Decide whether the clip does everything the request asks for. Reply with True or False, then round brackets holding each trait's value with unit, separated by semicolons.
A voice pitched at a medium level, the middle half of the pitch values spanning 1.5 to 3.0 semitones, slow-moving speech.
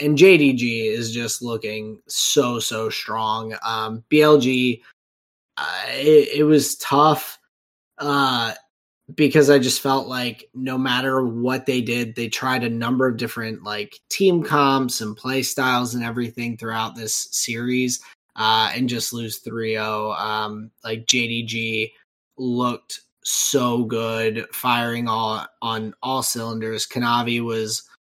False (120 Hz; 2.6 semitones; 130 wpm)